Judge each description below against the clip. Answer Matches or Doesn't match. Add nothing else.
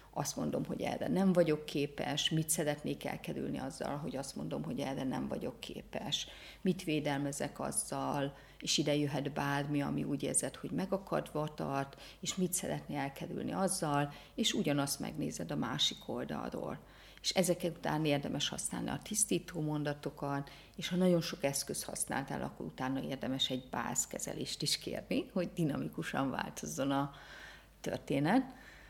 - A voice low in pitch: Doesn't match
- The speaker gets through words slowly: Doesn't match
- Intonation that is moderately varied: Matches